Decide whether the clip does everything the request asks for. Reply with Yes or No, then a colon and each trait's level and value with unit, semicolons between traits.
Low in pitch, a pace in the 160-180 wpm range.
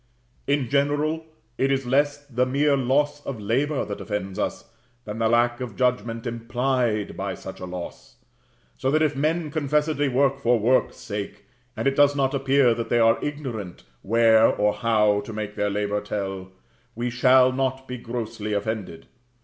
Yes: low, 120 Hz; average, 165 wpm